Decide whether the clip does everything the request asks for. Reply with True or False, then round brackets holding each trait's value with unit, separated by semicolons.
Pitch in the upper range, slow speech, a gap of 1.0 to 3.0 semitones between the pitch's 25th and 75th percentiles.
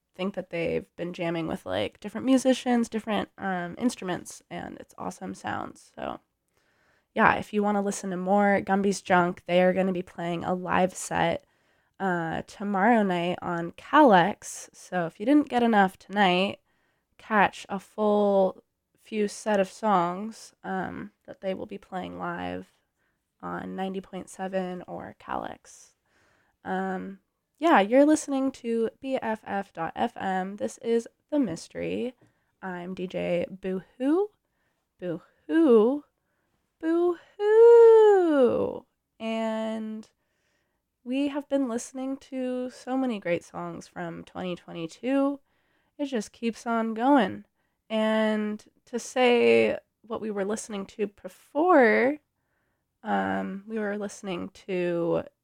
False (205 Hz; 120 wpm; 5.2 semitones)